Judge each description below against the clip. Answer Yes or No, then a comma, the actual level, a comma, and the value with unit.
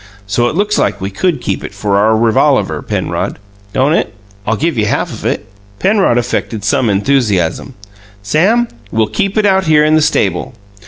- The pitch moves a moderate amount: No, wide, 8.2 semitones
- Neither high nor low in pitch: No, low, 125 Hz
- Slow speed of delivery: No, average, 180 wpm